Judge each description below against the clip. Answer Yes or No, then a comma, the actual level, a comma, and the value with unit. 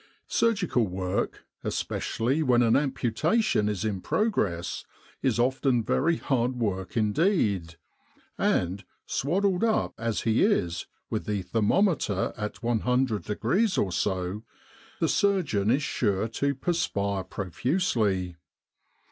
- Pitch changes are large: Yes, wide, 6.8 semitones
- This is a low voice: Yes, low, 115 Hz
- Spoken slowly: Yes, slow, 115 wpm